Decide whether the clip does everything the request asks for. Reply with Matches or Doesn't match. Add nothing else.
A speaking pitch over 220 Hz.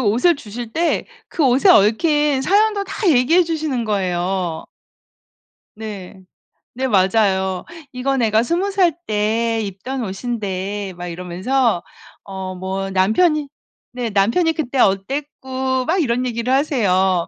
Matches